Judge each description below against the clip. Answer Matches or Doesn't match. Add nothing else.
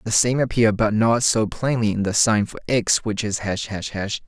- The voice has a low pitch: Matches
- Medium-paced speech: Doesn't match